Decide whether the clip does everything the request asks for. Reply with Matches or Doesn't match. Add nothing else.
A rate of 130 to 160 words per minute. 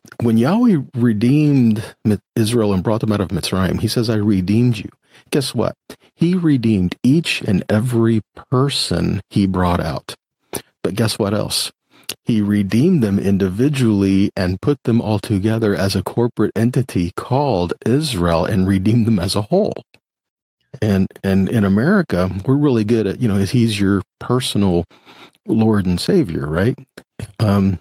Matches